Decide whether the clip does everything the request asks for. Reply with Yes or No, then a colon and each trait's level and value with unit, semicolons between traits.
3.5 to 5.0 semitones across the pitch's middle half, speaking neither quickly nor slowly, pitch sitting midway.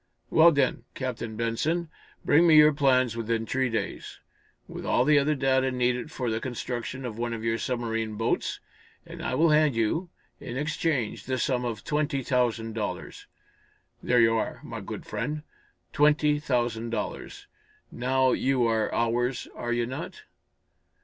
No: average, 3.8 semitones; average, 155 wpm; low, 125 Hz